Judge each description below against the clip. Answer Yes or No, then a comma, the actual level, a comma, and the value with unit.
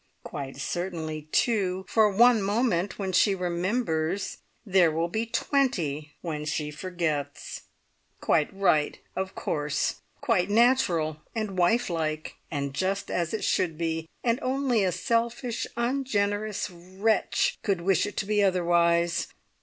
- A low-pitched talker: No, medium, 185 Hz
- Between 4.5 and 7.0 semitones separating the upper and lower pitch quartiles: Yes, average, 4.9 semitones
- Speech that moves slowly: Yes, slow, 130 wpm